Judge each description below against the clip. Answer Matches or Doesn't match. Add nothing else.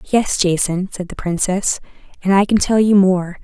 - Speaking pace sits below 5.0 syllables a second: Matches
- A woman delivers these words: Matches